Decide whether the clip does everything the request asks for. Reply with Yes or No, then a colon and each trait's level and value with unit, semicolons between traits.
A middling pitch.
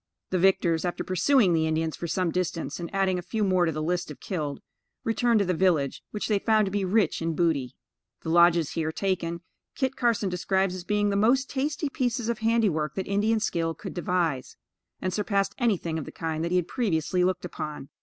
Yes: medium, 180 Hz